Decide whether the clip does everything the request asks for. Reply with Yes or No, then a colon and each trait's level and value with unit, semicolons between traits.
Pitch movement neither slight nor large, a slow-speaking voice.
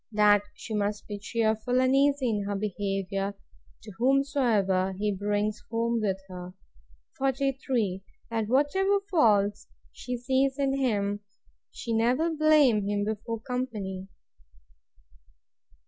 Yes: average, 4.6 semitones; slow, 115 wpm